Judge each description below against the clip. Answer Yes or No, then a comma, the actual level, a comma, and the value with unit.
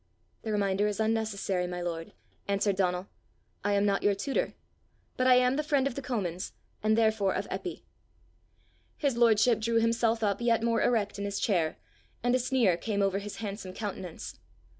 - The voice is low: No, high, 210 Hz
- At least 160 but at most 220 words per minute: Yes, average, 180 wpm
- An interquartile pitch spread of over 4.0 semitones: No, average, 2.9 semitones